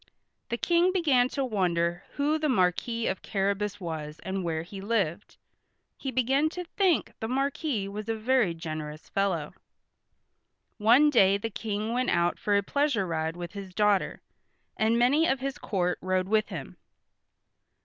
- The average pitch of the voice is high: Yes, high, 210 Hz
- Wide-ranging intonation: Yes, wide, 6.1 semitones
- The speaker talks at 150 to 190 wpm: Yes, average, 160 wpm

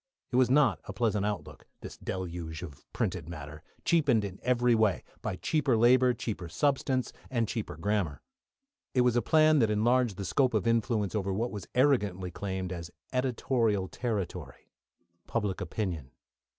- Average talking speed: Yes, average, 155 wpm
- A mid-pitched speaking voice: No, low, 110 Hz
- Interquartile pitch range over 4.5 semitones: Yes, average, 5.0 semitones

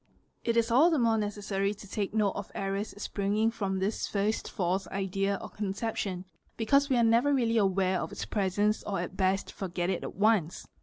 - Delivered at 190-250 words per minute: Yes, fast, 205 wpm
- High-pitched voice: Yes, high, 205 Hz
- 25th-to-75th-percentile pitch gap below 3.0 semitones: Yes, narrow, 2.6 semitones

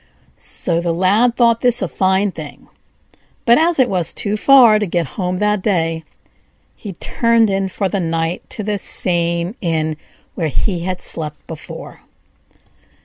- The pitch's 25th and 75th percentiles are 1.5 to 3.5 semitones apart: No, average, 4.0 semitones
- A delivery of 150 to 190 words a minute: Yes, average, 160 wpm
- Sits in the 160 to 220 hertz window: Yes, high, 190 Hz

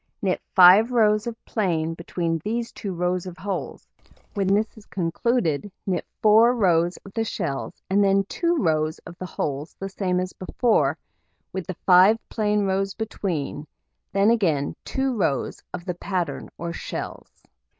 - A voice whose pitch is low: No, high, 190 Hz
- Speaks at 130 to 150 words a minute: No, average, 160 wpm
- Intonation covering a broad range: No, average, 3.7 semitones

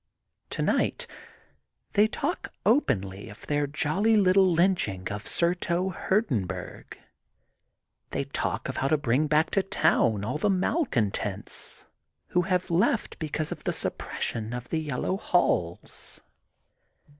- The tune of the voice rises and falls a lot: Yes, wide, 8.1 semitones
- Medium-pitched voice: Yes, medium, 155 Hz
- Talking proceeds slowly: Yes, slow, 120 wpm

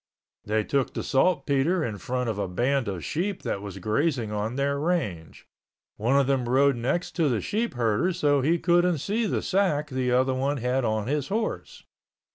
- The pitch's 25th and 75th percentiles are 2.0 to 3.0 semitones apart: No, wide, 5.6 semitones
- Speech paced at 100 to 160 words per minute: No, average, 185 wpm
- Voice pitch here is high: No, low, 135 Hz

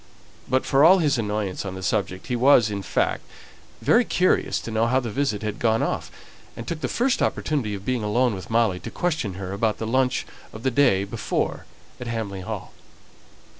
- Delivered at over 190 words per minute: Yes, average, 200 wpm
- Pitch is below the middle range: Yes, low, 115 Hz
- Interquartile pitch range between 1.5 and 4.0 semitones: No, average, 4.4 semitones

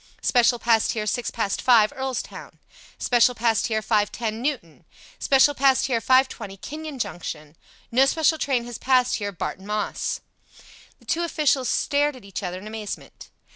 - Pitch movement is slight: No, average, 4.0 semitones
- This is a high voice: Yes, high, 240 Hz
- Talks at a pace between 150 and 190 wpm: Yes, average, 155 wpm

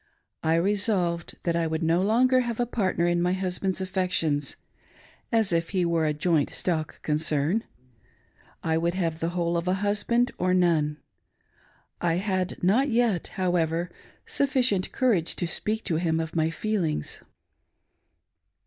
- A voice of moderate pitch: Yes, medium, 175 Hz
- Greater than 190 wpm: No, average, 155 wpm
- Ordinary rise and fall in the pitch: Yes, average, 3.7 semitones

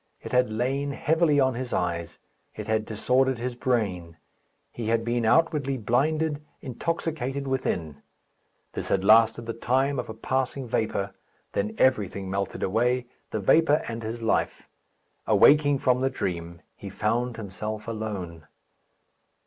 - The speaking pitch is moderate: No, low, 120 Hz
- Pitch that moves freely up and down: No, average, 3.8 semitones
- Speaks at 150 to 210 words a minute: No, average, 140 wpm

